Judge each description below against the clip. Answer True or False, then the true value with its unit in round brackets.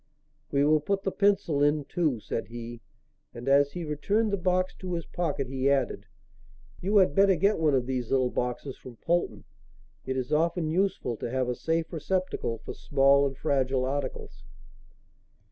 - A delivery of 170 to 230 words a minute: True (175 wpm)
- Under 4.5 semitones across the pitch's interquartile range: False (5.1 semitones)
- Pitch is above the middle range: False (145 Hz)